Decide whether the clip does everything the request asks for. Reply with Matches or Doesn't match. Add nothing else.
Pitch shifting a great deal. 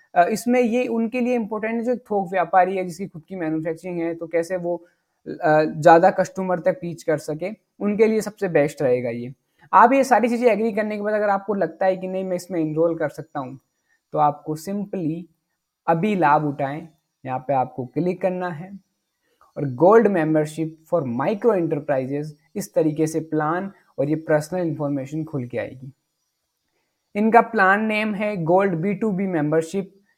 Doesn't match